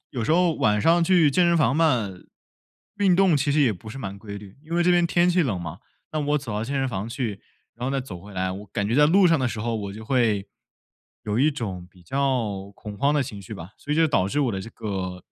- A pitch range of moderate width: No, wide, 6.7 semitones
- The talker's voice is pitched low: Yes, low, 120 Hz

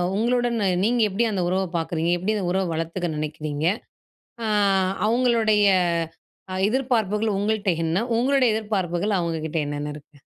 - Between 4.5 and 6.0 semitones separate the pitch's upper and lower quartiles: Yes, average, 5.3 semitones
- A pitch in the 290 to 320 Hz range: No, high, 200 Hz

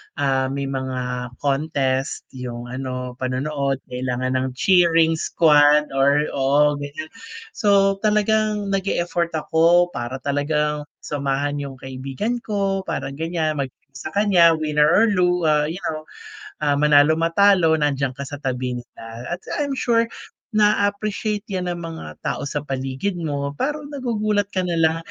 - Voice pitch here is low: No, medium, 150 Hz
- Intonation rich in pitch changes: Yes, wide, 5.8 semitones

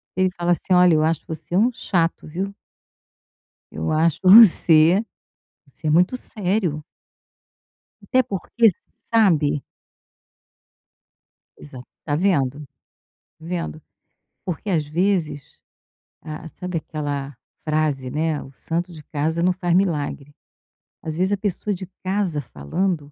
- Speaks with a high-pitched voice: No, medium, 165 Hz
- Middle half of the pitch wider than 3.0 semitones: Yes, average, 3.7 semitones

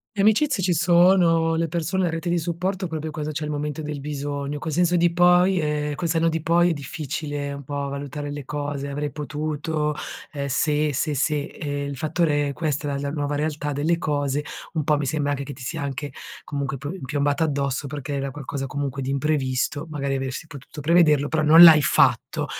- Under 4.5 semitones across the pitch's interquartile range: Yes, narrow, 2.4 semitones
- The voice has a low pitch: No, medium, 150 Hz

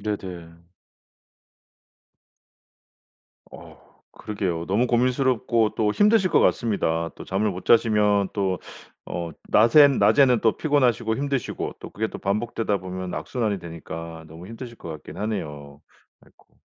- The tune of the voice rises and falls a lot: No, average, 4.9 semitones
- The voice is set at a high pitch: No, low, 105 Hz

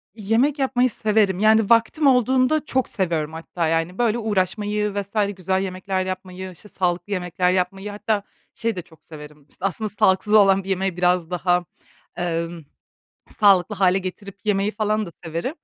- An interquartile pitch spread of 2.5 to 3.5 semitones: Yes, average, 3.1 semitones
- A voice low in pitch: No, high, 195 Hz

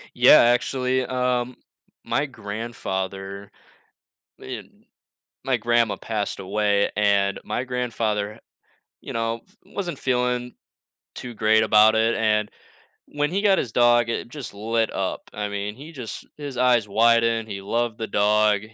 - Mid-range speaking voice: No, low, 115 Hz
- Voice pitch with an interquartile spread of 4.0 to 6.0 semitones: No, average, 2.9 semitones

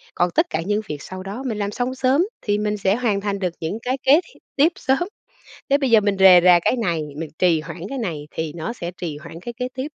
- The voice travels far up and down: Yes, wide, 6.3 semitones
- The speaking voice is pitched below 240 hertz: Yes, high, 205 Hz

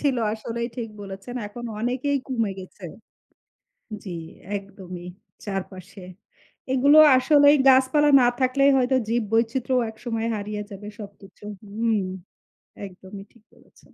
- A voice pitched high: Yes, high, 230 Hz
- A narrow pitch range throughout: No, average, 4.3 semitones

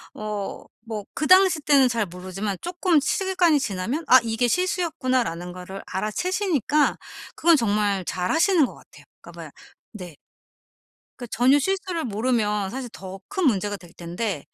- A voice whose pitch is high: Yes, high, 240 Hz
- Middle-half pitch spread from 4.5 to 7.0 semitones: No, wide, 8.4 semitones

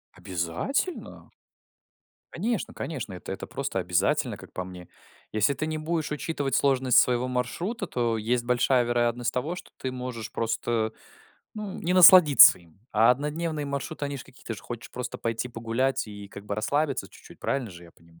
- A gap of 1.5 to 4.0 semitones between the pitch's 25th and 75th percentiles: No, average, 4.9 semitones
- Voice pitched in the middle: No, low, 125 Hz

